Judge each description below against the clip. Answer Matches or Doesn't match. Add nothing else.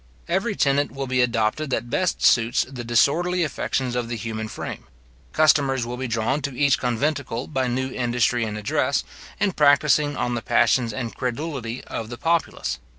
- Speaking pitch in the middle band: Doesn't match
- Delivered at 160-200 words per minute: Matches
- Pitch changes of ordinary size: Matches